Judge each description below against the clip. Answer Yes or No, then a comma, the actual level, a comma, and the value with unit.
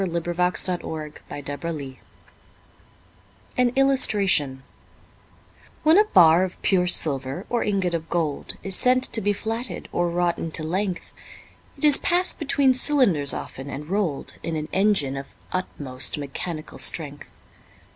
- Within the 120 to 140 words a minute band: Yes, slow, 135 wpm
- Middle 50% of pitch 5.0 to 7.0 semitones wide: Yes, wide, 5.6 semitones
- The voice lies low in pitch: No, medium, 175 Hz